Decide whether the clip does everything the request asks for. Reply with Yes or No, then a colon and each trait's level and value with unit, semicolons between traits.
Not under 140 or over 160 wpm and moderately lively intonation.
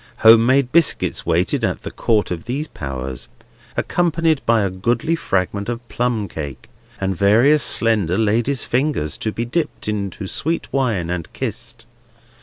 No: average, 150 wpm; wide, 5.8 semitones